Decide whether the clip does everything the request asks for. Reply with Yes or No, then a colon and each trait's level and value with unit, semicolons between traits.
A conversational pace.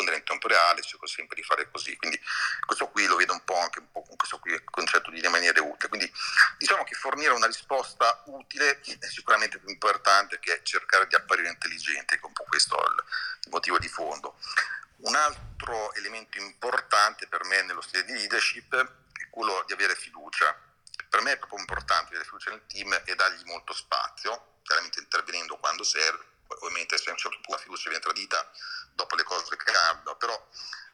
No: fast, 180 wpm